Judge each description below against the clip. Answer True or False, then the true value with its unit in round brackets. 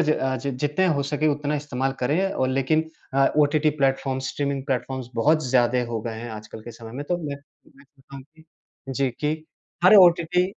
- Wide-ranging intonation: False (2.7 semitones)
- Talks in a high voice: False (140 Hz)